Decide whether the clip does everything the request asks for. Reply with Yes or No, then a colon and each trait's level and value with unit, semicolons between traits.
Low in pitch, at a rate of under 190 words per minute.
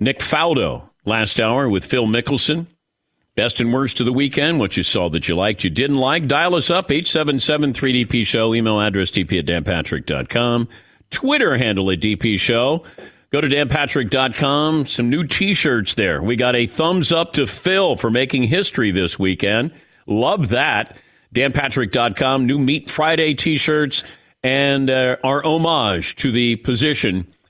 Yes: low, 130 Hz; average, 155 wpm